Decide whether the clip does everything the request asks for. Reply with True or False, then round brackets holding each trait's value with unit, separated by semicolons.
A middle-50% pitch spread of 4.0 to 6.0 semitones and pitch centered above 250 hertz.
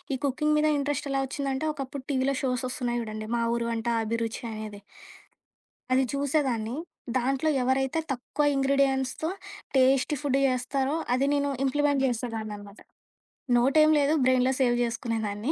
False (2.7 semitones; 260 Hz)